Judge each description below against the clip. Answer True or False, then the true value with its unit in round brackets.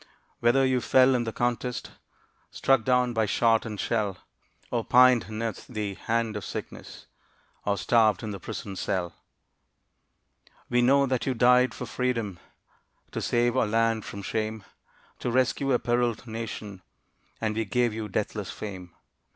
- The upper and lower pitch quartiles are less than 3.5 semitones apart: True (2.6 semitones)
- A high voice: False (115 Hz)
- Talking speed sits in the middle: True (150 wpm)